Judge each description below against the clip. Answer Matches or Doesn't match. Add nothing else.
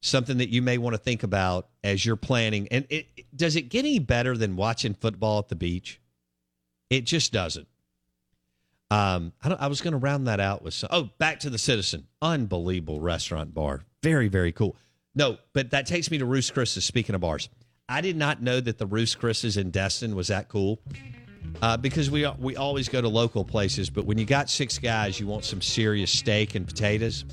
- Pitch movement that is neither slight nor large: Doesn't match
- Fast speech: Matches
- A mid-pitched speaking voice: Doesn't match